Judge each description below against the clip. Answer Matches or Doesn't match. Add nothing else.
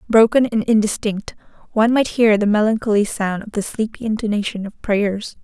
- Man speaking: Doesn't match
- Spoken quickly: Doesn't match